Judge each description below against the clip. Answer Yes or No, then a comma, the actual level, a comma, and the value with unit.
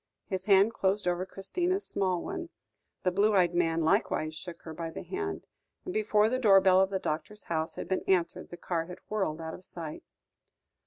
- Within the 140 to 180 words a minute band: No, average, 200 wpm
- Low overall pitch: No, high, 190 Hz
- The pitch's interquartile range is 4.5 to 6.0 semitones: No, average, 3.8 semitones